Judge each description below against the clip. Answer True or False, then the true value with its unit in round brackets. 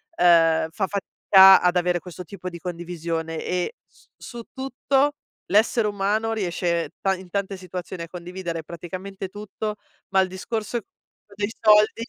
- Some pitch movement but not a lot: True (3.1 semitones)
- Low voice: False (190 Hz)